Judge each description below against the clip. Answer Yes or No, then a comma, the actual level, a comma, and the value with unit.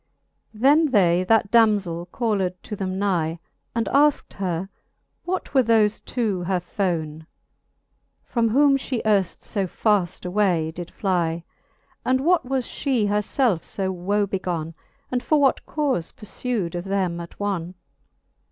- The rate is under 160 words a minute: Yes, average, 145 wpm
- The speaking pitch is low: No, high, 200 Hz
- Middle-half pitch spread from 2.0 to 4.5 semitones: No, average, 5.0 semitones